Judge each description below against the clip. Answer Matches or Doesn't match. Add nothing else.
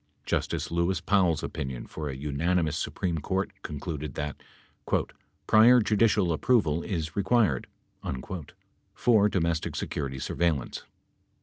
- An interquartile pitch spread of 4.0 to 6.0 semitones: Matches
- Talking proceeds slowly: Matches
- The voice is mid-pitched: Doesn't match